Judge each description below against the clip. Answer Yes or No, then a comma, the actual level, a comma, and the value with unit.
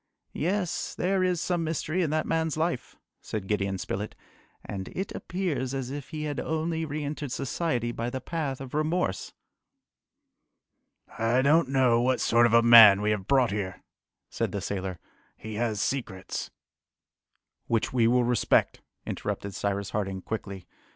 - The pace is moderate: Yes, average, 160 wpm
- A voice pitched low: Yes, low, 125 Hz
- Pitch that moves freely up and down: Yes, wide, 6.7 semitones